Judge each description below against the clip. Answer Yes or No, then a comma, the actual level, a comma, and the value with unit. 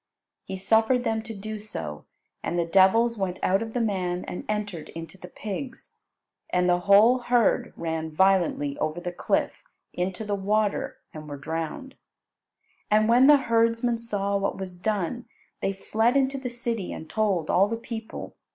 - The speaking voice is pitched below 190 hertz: No, high, 205 Hz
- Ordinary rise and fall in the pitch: Yes, average, 4.3 semitones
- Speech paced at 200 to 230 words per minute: No, average, 170 wpm